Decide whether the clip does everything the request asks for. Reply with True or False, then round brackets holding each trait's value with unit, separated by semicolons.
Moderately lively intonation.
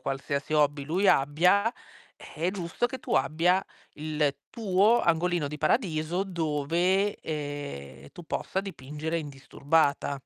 True (4.1 semitones)